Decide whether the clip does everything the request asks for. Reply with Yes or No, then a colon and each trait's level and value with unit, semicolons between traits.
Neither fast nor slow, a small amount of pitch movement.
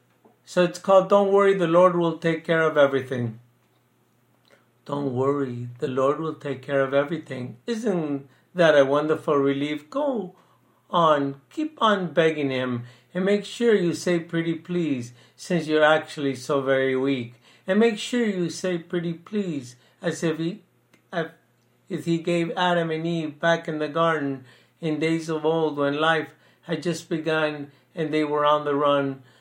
No: average, 165 wpm; average, 3.8 semitones